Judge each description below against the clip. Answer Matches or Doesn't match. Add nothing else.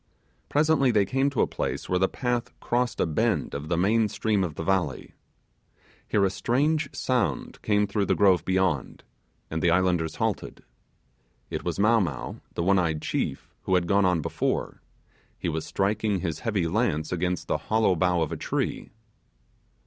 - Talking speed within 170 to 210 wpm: Matches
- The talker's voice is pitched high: Doesn't match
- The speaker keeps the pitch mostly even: Doesn't match